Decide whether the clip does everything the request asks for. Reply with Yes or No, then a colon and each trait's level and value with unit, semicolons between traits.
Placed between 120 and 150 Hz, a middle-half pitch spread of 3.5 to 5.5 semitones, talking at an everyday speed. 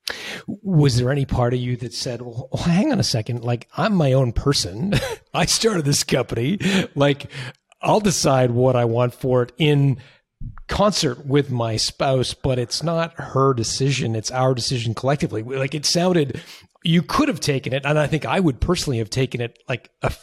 Yes: low, 135 Hz; average, 4.3 semitones; average, 185 wpm